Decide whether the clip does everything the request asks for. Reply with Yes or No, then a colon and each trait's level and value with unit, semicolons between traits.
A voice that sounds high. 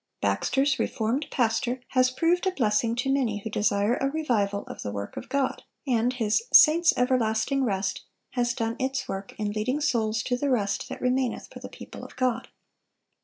Yes: high, 245 Hz